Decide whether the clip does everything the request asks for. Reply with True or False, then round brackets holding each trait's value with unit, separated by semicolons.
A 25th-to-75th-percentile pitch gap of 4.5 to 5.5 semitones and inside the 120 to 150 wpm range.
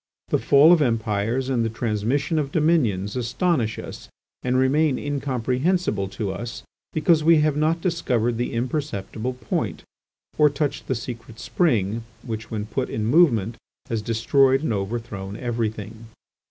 True (4.8 semitones; 140 wpm)